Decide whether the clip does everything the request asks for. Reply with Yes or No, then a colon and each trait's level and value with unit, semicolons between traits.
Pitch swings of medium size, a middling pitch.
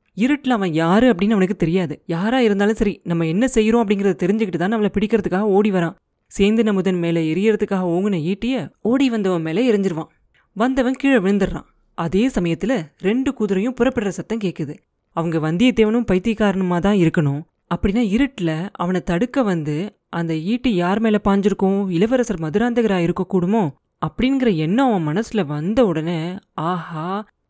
No: average, 4.6 semitones; high, 200 Hz